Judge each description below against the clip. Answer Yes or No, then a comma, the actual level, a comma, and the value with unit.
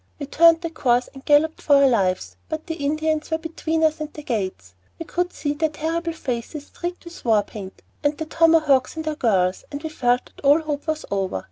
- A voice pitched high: Yes, very high, 300 Hz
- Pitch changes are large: No, average, 4.4 semitones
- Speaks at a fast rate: Yes, fast, 220 wpm